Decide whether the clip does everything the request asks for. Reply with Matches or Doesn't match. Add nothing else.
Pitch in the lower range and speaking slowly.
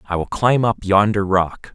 Doesn't match